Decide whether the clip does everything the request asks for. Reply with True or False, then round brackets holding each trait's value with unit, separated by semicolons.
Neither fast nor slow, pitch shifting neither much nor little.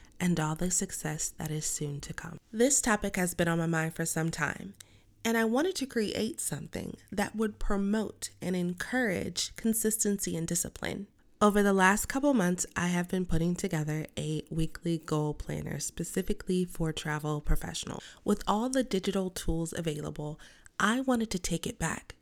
True (170 wpm; 4.4 semitones)